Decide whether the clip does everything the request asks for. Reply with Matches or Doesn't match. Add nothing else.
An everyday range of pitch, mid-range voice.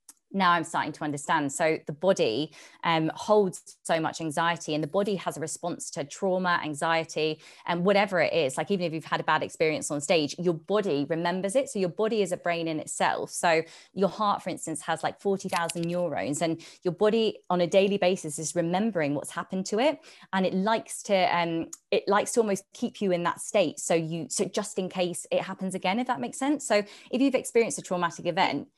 Matches